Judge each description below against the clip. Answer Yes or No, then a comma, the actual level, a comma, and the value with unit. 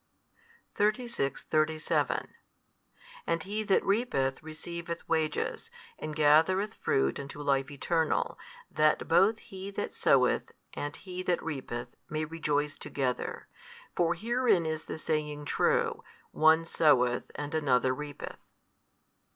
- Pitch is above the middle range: No, medium, 155 Hz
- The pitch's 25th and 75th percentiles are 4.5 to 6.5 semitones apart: No, average, 3.4 semitones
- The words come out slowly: Yes, slow, 115 wpm